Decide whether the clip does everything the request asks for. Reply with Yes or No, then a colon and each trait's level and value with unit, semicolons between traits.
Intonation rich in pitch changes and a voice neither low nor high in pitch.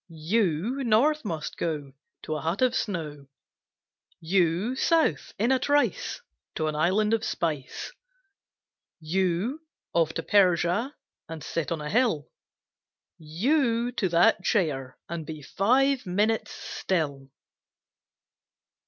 Yes: wide, 6.7 semitones; medium, 180 Hz